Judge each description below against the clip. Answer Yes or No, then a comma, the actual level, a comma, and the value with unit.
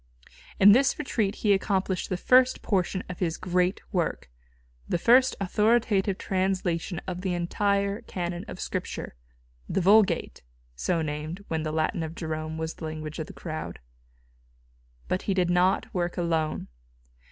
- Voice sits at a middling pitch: Yes, medium, 180 Hz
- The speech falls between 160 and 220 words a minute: No, average, 150 wpm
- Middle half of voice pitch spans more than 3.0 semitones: Yes, average, 3.4 semitones